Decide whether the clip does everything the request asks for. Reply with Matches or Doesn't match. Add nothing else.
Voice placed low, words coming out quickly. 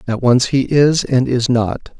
Matches